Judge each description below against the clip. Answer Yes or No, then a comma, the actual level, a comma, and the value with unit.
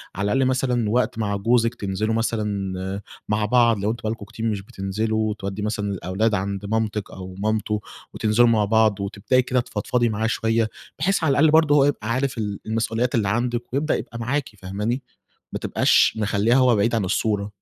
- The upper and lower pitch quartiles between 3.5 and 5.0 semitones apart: No, average, 2.8 semitones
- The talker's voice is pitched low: Yes, low, 110 Hz